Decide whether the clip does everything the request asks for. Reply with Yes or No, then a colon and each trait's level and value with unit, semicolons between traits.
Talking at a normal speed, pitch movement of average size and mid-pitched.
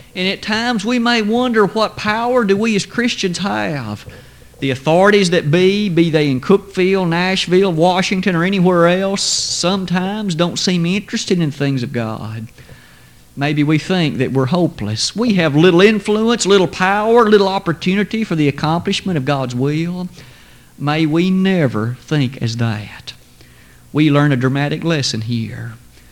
No: average, 150 wpm; wide, 6.5 semitones; medium, 170 Hz